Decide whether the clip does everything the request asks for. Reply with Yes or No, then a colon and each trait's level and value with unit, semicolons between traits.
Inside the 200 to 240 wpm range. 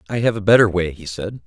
No: fast, 285 wpm